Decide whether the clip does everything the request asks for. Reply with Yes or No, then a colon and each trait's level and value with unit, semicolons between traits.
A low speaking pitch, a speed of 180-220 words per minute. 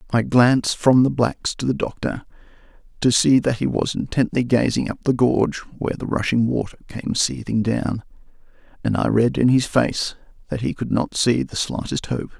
Yes: low, 120 Hz; average, 190 wpm